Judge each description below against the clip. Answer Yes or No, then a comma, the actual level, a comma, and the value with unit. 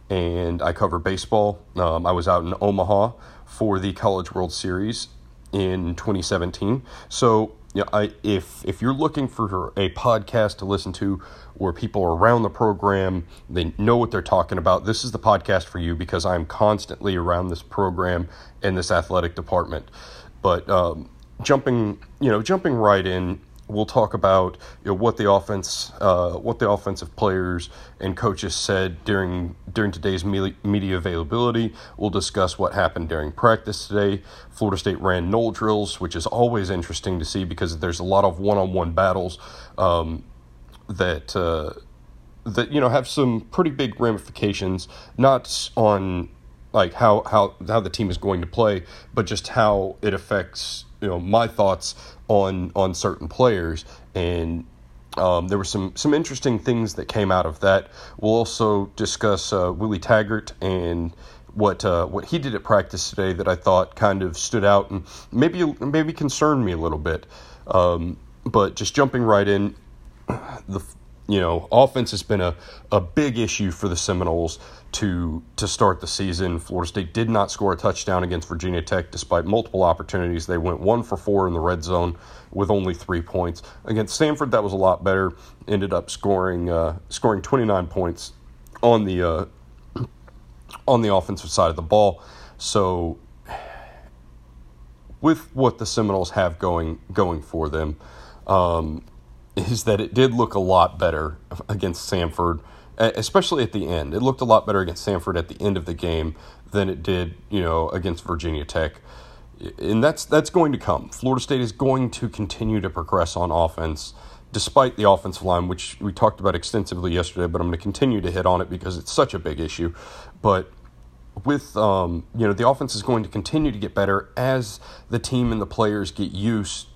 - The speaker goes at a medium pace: Yes, average, 180 wpm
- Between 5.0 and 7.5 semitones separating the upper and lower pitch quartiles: No, average, 3.8 semitones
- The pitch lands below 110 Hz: Yes, very low, 95 Hz